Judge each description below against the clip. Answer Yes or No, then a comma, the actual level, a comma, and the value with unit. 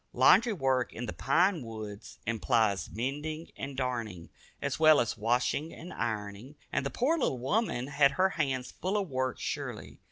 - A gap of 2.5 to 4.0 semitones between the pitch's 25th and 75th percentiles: No, average, 5.3 semitones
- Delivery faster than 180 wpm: No, average, 165 wpm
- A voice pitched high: No, low, 130 Hz